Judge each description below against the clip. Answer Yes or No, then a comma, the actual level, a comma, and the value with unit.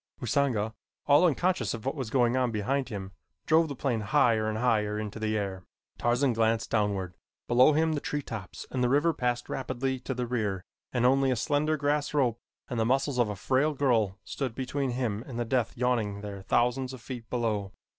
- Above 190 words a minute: Yes, average, 200 wpm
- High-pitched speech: No, low, 125 Hz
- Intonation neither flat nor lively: Yes, average, 3.8 semitones